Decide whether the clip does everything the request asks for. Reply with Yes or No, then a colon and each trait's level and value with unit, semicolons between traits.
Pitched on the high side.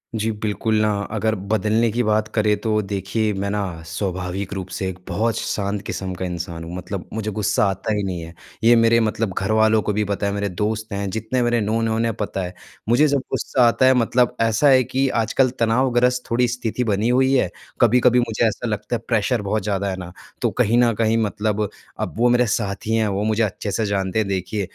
No: low, 110 Hz